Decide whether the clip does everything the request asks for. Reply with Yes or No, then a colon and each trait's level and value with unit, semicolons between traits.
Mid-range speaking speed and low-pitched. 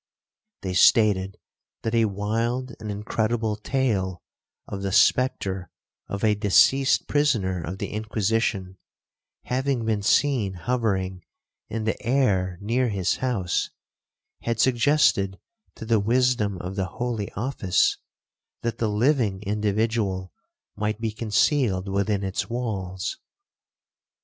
No: slow, 115 wpm; low, 105 Hz